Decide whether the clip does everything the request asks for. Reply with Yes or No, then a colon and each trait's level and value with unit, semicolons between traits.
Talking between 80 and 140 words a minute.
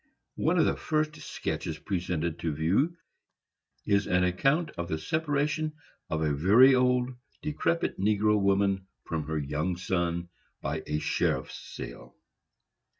Yes: slow, 135 wpm